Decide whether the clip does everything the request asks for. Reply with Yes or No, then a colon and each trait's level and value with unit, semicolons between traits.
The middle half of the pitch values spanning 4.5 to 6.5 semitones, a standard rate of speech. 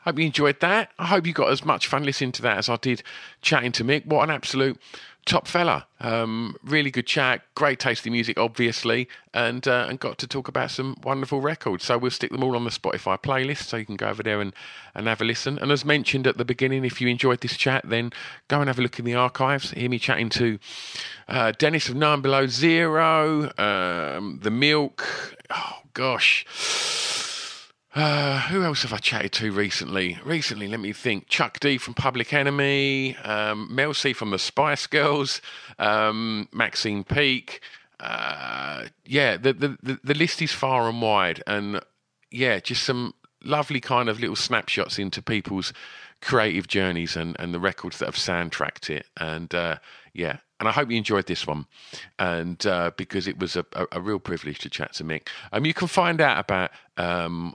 Yes: average, 5.1 semitones; average, 195 wpm